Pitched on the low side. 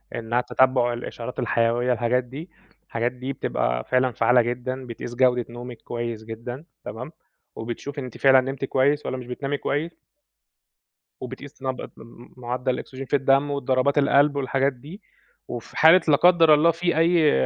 Yes: low, 130 Hz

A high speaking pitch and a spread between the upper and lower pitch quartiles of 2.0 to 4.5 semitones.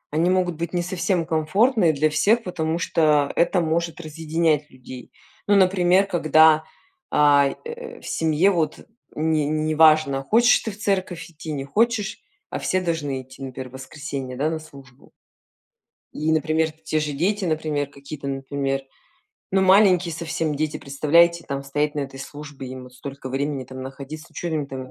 No: medium, 155 Hz; average, 3.5 semitones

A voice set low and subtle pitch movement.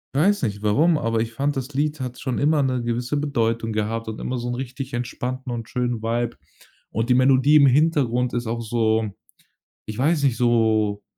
No: low, 125 Hz; average, 3.1 semitones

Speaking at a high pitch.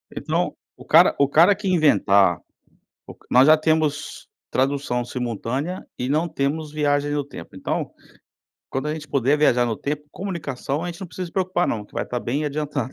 No: medium, 145 Hz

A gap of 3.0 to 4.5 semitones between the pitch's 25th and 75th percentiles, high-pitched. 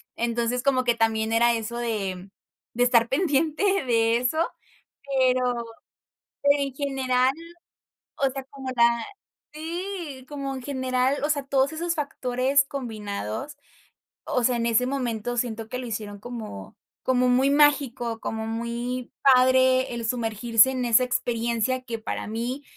No: narrow, 2.6 semitones; very high, 250 Hz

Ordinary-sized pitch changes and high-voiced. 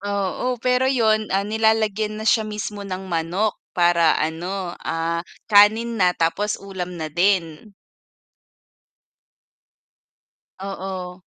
Yes: average, 3.6 semitones; high, 195 Hz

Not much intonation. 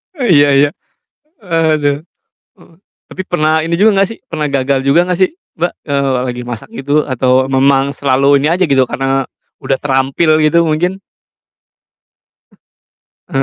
No: average, 3.5 semitones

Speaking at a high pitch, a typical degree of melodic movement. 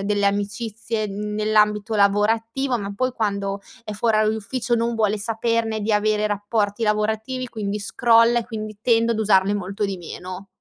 No: high, 215 Hz; narrow, 1.9 semitones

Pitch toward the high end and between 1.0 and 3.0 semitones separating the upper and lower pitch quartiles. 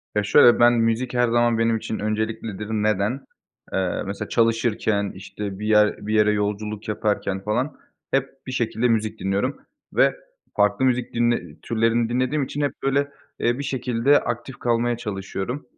No: low, 115 Hz; narrow, 2.6 semitones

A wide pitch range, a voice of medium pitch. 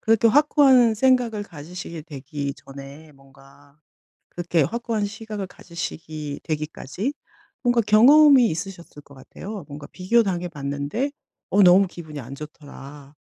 Yes: wide, 7.2 semitones; medium, 175 Hz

